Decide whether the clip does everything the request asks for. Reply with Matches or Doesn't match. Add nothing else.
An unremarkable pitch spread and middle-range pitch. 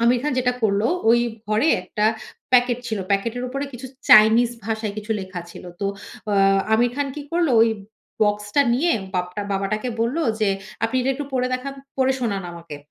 Doesn't match